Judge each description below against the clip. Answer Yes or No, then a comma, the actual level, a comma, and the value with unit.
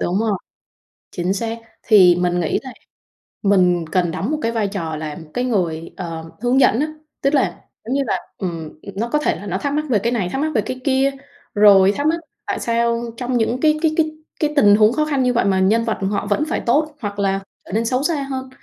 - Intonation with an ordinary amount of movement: No, wide, 5.9 semitones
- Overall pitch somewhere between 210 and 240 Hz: Yes, high, 225 Hz